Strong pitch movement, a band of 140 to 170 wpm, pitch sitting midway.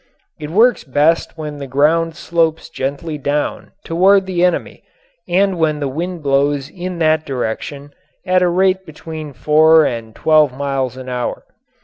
No: average, 3.4 semitones; average, 150 wpm; medium, 155 Hz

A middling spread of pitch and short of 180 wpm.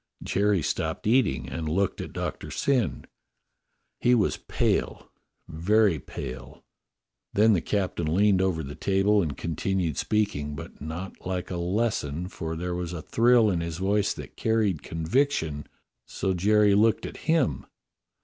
Yes: average, 4.5 semitones; average, 150 wpm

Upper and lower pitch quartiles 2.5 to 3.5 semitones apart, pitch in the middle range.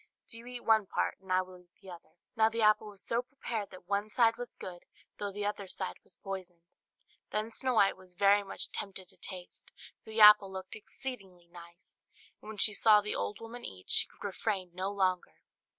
No: average, 2.9 semitones; high, 200 Hz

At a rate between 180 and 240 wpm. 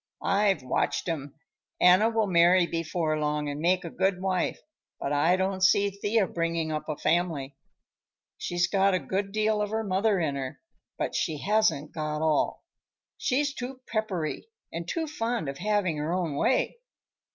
No: average, 165 wpm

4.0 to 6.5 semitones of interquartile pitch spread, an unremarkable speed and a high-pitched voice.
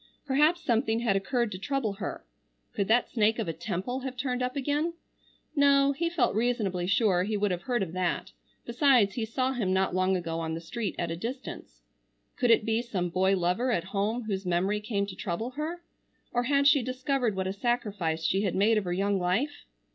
No: average, 5.1 semitones; fast, 210 wpm; high, 220 Hz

